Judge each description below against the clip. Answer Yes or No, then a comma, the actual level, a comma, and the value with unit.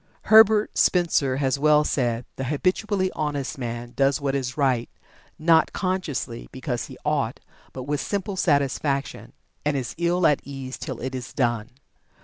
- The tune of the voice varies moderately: Yes, average, 4.6 semitones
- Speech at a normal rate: Yes, average, 150 wpm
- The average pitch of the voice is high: No, medium, 140 Hz